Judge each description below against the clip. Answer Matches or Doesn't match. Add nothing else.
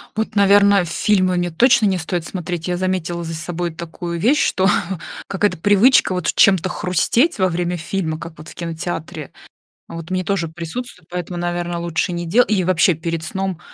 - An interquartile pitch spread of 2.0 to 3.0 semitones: Matches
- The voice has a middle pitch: Matches